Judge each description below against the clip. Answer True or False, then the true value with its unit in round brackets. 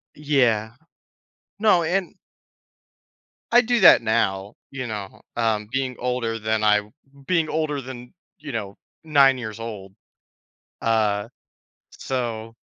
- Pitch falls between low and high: False (120 Hz)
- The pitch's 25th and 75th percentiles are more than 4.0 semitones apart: True (4.6 semitones)